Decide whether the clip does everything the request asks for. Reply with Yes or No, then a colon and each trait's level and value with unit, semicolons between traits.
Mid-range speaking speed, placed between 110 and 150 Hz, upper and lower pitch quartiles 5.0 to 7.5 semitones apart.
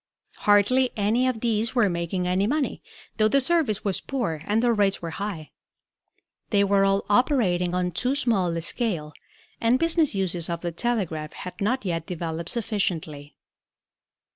No: average, 160 wpm; high, 200 Hz; wide, 5.4 semitones